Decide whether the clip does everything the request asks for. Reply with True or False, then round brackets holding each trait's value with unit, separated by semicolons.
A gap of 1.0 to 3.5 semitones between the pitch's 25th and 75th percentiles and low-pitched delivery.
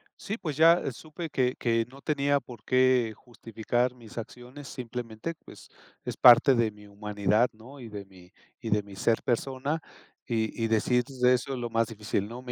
True (2.9 semitones; 120 Hz)